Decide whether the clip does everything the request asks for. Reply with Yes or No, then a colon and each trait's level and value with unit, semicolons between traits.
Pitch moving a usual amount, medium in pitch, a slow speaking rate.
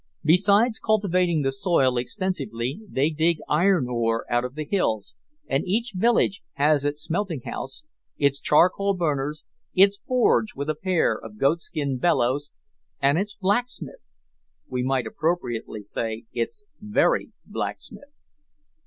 No: wide, 6.7 semitones; medium, 155 Hz; slow, 130 wpm